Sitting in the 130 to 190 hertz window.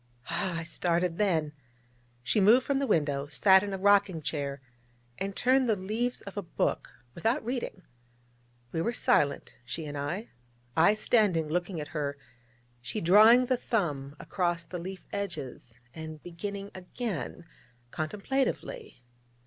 Yes: medium, 185 Hz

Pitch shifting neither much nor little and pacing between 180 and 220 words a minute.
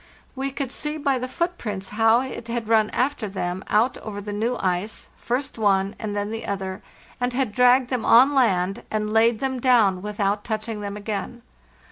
Yes: average, 3.6 semitones; average, 185 wpm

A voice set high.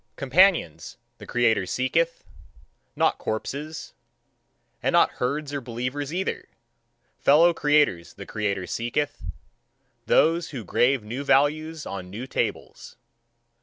No: medium, 140 Hz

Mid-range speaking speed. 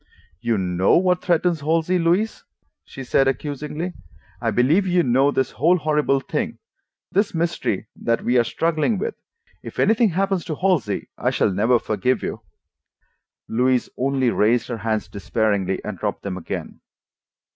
Yes: average, 150 wpm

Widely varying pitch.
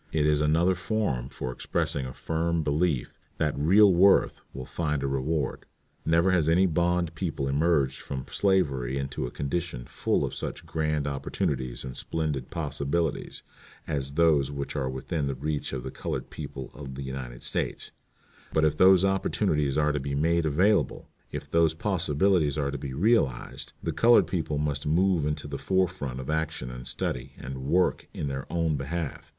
No: average, 3.7 semitones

